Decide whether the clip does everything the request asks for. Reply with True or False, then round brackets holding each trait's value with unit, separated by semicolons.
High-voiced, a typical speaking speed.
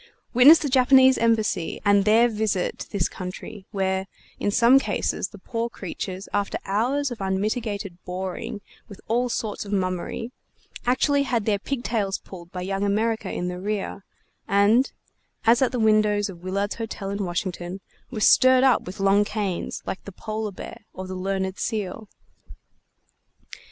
True (205 Hz; 155 wpm)